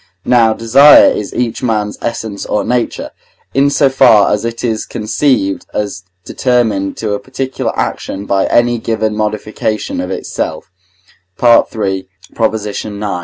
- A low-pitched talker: Yes, low, 110 Hz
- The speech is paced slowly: Yes, slow, 130 wpm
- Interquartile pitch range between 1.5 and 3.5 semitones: Yes, average, 2.7 semitones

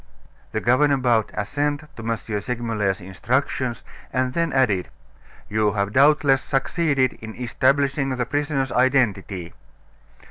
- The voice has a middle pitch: No, low, 125 Hz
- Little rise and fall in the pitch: No, average, 4.2 semitones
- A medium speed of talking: No, slow, 115 wpm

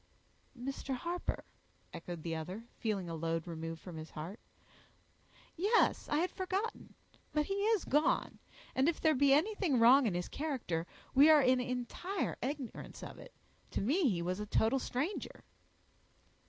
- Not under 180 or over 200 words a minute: No, average, 155 wpm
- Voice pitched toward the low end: No, very high, 255 Hz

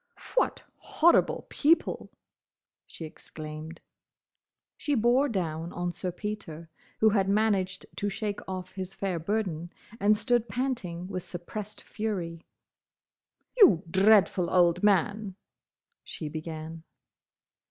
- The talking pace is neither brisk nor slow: No, slow, 110 wpm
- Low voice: No, high, 190 Hz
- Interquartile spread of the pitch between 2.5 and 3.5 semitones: No, average, 4.0 semitones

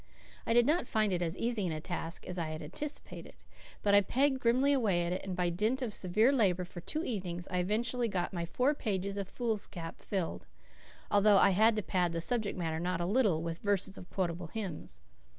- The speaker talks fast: Yes, fast, 210 wpm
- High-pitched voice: Yes, high, 195 Hz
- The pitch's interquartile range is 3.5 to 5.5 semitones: Yes, average, 4.5 semitones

